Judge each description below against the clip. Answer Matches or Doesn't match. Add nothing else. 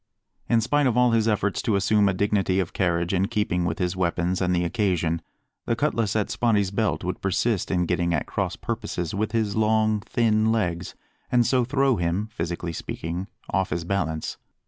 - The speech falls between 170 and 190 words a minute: Matches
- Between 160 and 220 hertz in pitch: Doesn't match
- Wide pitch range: Doesn't match